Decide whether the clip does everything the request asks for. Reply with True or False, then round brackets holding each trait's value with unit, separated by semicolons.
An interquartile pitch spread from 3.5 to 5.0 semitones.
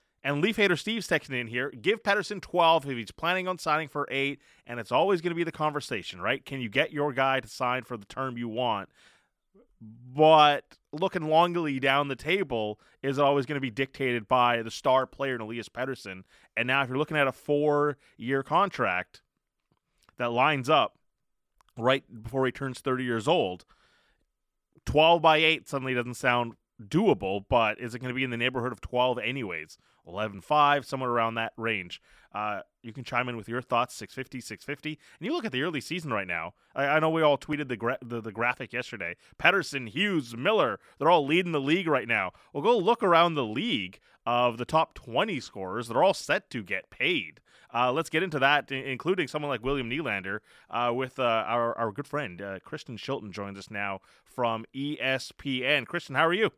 True (3.9 semitones)